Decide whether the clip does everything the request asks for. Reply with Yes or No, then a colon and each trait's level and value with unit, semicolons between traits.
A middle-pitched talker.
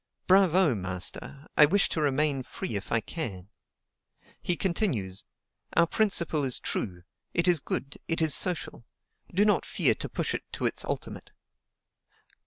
Yes: medium, 150 Hz